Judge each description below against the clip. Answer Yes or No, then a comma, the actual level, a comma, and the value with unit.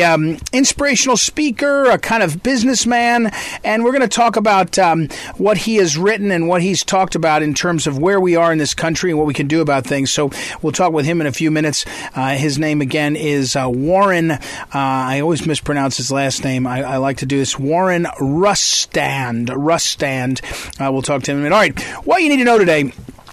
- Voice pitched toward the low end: No, medium, 160 Hz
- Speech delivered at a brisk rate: Yes, fast, 225 wpm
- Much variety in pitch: Yes, wide, 6.0 semitones